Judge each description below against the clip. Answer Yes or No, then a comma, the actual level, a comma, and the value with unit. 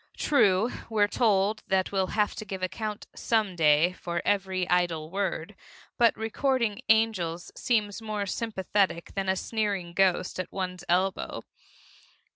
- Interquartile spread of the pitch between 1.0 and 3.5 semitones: Yes, average, 2.9 semitones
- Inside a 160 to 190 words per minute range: No, slow, 135 wpm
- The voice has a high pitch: Yes, high, 195 Hz